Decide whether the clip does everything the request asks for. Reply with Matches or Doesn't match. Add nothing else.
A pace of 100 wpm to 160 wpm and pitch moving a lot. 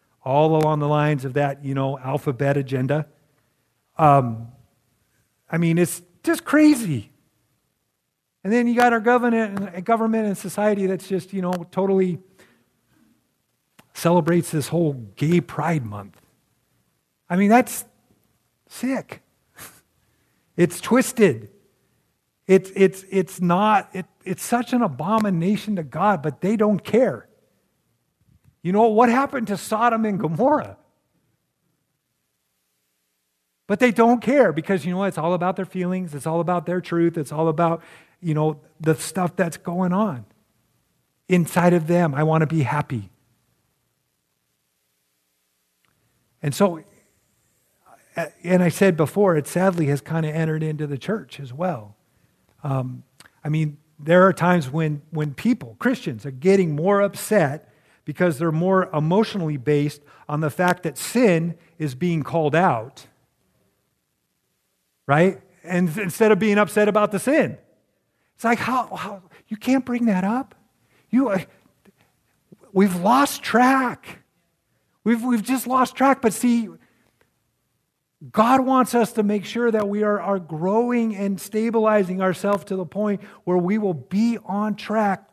Matches